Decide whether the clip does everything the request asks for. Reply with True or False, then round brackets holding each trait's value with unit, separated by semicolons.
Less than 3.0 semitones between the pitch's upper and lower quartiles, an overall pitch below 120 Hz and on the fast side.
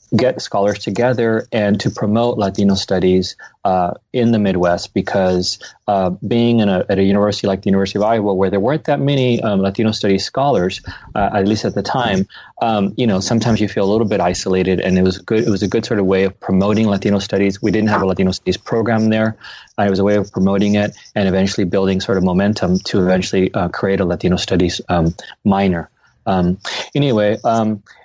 True (2.4 semitones; 100 Hz; 210 wpm)